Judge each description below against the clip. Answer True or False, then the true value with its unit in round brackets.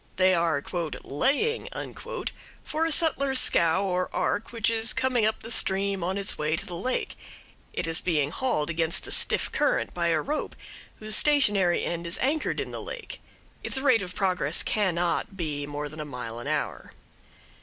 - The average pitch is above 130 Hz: True (185 Hz)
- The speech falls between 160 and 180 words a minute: True (175 wpm)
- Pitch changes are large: True (6.0 semitones)